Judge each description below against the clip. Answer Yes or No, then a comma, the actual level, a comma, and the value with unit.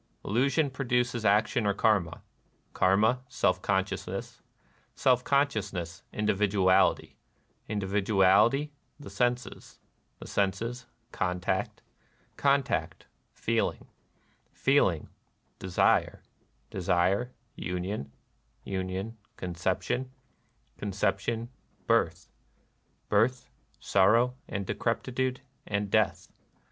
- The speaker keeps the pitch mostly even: No, average, 4.4 semitones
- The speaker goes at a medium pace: No, slow, 80 wpm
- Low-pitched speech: Yes, low, 105 Hz